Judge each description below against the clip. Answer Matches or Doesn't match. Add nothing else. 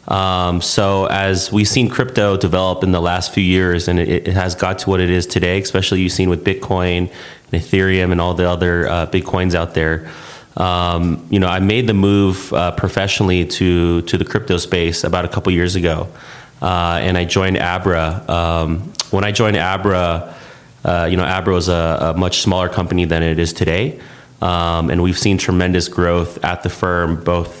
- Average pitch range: Doesn't match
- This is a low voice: Matches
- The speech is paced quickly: Matches